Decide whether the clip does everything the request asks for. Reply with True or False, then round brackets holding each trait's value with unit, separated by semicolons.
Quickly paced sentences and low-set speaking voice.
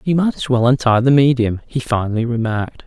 True (210 wpm; 125 Hz)